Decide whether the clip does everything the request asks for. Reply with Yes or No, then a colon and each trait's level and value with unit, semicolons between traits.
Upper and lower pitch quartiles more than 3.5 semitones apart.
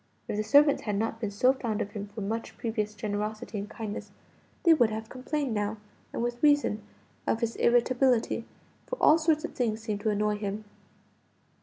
No: average, 3.2 semitones